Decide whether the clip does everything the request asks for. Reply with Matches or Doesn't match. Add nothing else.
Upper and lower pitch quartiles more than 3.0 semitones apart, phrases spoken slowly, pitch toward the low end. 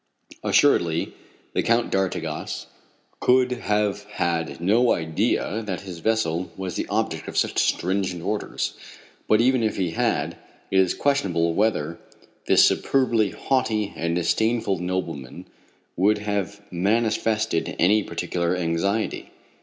Matches